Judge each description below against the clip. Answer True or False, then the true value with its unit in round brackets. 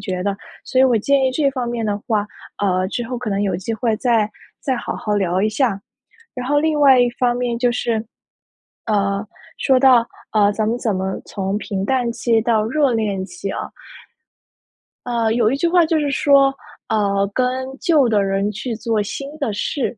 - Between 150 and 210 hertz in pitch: False (230 Hz)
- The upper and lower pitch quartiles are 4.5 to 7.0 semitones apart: False (4.1 semitones)